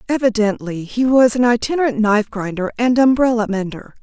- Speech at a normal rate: Yes, average, 150 wpm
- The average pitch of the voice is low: No, high, 225 Hz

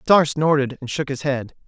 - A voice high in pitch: No, medium, 140 Hz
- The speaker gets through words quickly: Yes, fast, 215 wpm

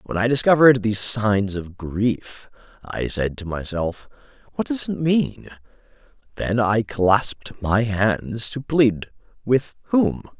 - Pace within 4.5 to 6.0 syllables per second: No, 3.8 syllables/s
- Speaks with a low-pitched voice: Yes, low, 115 Hz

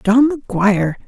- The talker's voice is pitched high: Yes, high, 225 Hz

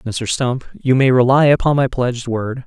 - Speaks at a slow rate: No, fast, 205 wpm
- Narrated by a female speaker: No, male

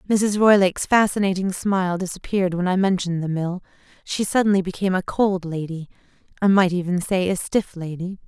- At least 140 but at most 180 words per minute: Yes, average, 160 wpm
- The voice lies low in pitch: No, medium, 185 Hz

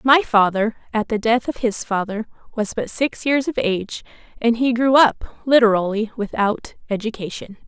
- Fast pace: No, average, 165 wpm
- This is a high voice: Yes, high, 225 Hz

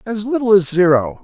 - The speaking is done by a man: Yes, male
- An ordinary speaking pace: Yes, average, 195 wpm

